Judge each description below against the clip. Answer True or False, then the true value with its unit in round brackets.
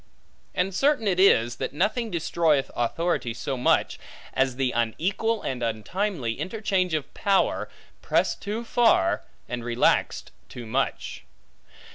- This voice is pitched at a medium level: True (165 Hz)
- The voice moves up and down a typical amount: False (8.7 semitones)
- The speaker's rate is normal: False (125 wpm)